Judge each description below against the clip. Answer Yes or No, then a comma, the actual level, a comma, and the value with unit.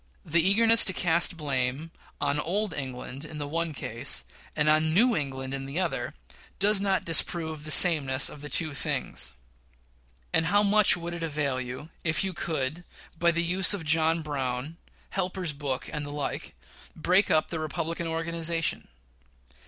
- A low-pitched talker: No, medium, 160 Hz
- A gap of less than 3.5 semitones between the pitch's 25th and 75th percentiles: Yes, average, 3.1 semitones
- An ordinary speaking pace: Yes, average, 165 wpm